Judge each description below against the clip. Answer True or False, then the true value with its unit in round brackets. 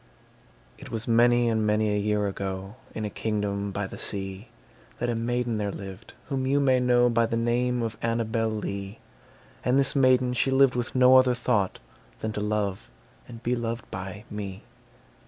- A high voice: False (115 Hz)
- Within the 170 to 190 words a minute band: True (180 wpm)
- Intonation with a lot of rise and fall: False (3.0 semitones)